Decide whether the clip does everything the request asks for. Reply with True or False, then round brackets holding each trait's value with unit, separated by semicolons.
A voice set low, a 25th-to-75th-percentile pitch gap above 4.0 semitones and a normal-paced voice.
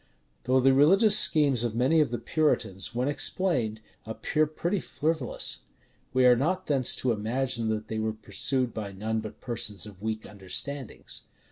True (125 Hz; 4.8 semitones; 160 wpm)